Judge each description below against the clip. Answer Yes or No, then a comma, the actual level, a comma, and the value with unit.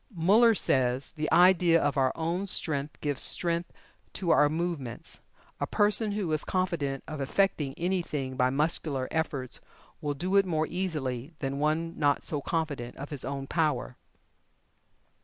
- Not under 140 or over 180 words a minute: Yes, average, 150 wpm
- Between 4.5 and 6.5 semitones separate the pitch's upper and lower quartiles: No, average, 4.0 semitones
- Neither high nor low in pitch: Yes, medium, 155 Hz